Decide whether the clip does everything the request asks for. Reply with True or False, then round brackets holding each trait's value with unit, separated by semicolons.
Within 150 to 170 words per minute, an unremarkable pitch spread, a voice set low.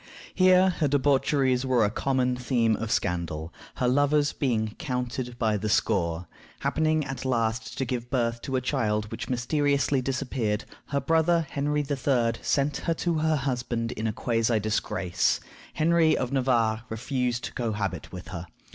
True (155 wpm; 4.1 semitones; 125 Hz)